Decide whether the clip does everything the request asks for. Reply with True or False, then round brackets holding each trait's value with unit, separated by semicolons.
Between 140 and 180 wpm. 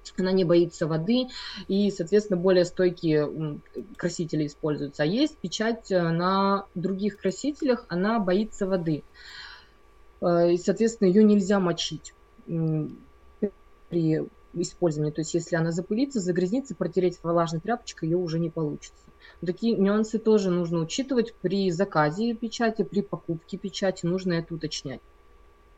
False (125 wpm)